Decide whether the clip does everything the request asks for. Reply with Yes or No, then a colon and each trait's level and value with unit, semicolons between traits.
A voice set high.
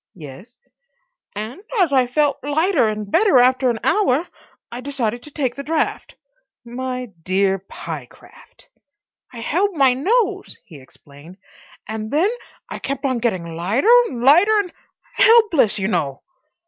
Yes: very high, 255 Hz